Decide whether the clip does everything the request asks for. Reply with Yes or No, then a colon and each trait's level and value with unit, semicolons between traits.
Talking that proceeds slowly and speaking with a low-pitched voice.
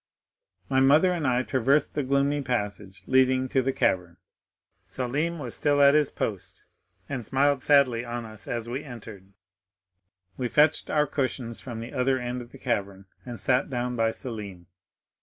No: average, 165 wpm; low, 125 Hz